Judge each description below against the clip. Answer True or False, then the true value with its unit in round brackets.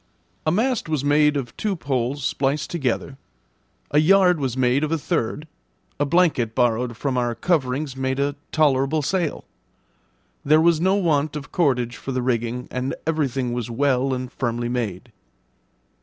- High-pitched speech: False (135 Hz)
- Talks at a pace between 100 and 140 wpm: False (155 wpm)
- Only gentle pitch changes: False (3.7 semitones)